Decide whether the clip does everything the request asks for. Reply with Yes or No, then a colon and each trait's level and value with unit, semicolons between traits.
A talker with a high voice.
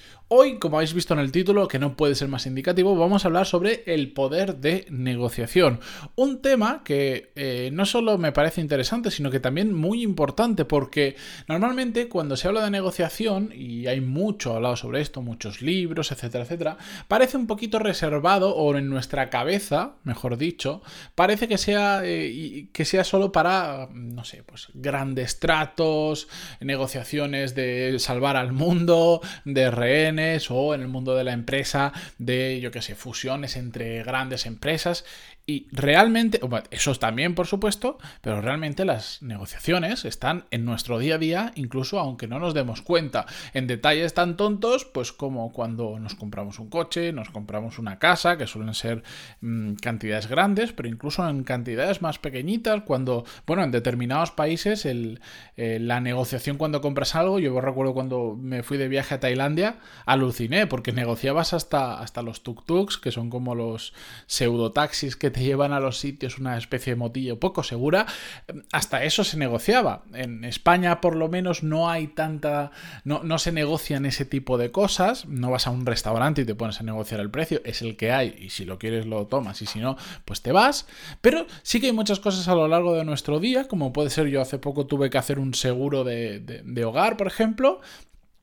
No: medium, 140 Hz